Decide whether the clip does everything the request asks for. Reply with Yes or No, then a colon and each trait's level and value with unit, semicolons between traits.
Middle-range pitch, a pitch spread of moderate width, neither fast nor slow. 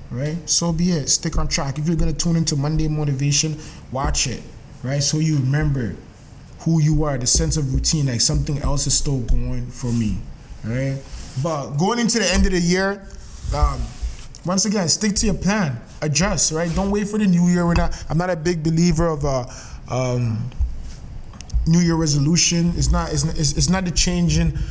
Yes: medium, 155 Hz; average, 3.9 semitones; average, 195 wpm